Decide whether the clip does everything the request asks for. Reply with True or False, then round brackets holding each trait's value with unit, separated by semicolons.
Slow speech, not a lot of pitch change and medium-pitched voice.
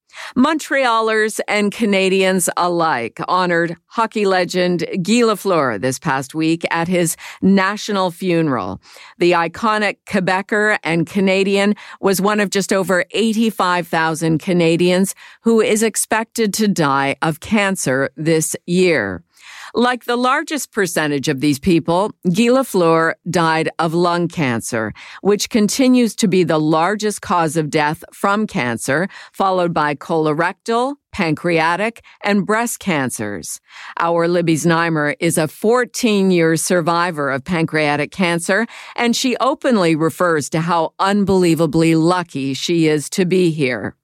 False (125 wpm; 4.4 semitones; 180 Hz)